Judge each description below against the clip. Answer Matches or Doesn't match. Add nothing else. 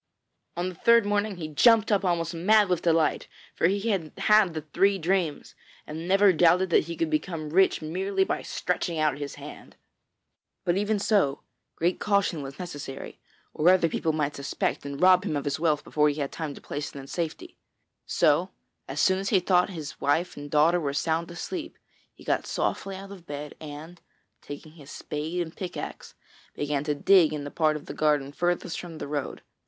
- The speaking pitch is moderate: Matches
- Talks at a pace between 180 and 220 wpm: Matches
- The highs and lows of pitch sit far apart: Doesn't match